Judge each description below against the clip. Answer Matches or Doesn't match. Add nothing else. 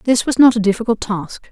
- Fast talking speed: Matches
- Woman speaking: Matches